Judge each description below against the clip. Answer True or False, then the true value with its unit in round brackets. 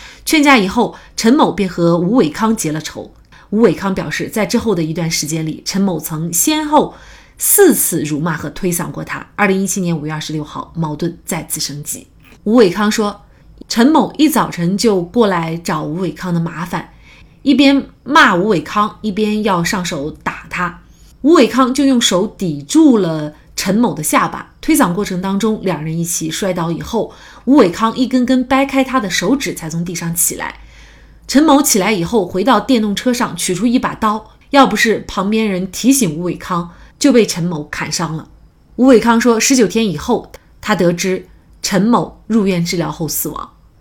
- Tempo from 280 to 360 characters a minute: False (265 characters per minute)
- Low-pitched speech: False (195 Hz)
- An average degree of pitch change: False (5.8 semitones)